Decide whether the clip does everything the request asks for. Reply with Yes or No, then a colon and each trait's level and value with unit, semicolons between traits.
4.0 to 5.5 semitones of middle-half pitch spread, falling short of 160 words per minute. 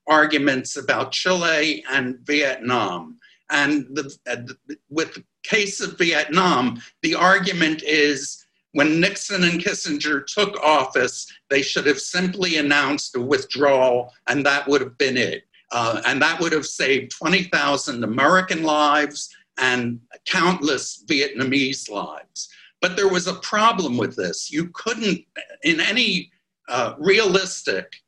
Yes: average, 5.0 semitones; slow, 135 wpm